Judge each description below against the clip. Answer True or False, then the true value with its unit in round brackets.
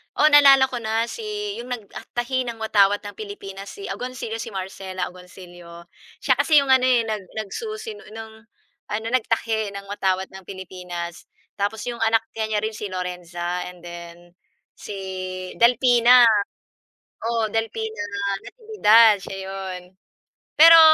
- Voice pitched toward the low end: False (220 Hz)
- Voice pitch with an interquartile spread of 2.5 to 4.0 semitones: False (4.5 semitones)